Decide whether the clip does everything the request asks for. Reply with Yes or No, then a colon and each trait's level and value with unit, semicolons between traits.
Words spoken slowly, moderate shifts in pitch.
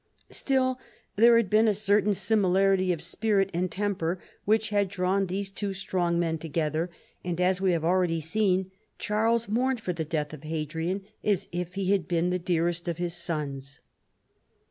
No: average, 170 wpm; average, 3.3 semitones